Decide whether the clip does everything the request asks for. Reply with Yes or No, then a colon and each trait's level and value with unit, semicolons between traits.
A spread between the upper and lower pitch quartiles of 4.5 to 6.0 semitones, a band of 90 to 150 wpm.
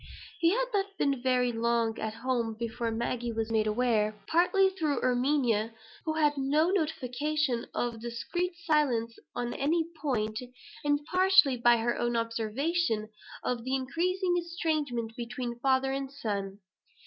Yes: average, 5.1 semitones; average, 140 wpm